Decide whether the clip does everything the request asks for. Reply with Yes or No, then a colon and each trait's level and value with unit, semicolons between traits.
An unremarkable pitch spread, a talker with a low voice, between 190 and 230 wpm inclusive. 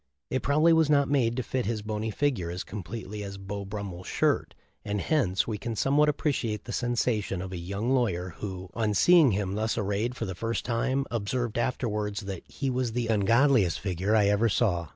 Yes: average, 4.0 semitones; low, 110 Hz; average, 195 wpm